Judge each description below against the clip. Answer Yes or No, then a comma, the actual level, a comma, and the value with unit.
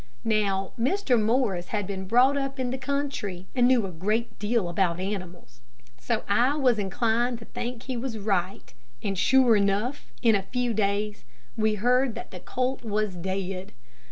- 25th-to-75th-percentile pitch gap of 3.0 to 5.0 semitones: Yes, average, 4.4 semitones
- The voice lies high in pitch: Yes, high, 215 Hz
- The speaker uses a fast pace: No, average, 170 wpm